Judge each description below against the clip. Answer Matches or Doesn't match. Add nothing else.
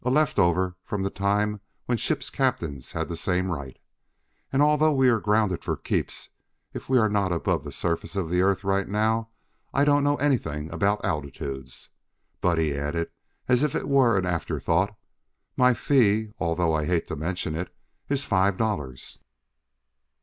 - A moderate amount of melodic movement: Doesn't match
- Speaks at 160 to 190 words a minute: Matches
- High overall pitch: Doesn't match